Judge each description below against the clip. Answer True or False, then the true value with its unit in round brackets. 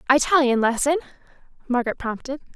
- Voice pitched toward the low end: False (265 Hz)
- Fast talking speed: False (95 wpm)